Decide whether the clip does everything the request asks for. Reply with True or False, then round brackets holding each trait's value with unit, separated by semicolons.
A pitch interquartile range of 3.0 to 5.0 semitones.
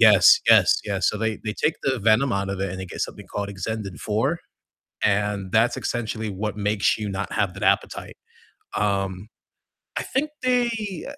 False (2.6 semitones)